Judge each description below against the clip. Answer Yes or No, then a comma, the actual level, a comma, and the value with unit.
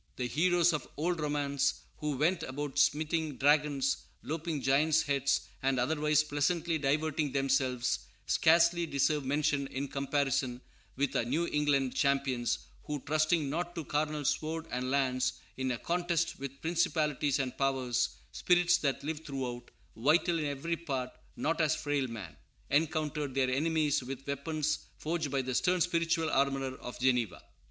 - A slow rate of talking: No, average, 145 wpm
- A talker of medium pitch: Yes, medium, 145 Hz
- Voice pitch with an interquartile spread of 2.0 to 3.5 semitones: Yes, average, 2.9 semitones